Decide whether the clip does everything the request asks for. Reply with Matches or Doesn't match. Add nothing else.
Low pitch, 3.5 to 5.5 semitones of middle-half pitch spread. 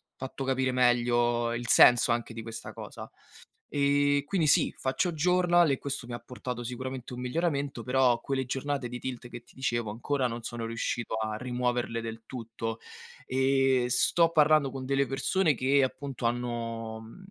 Doesn't match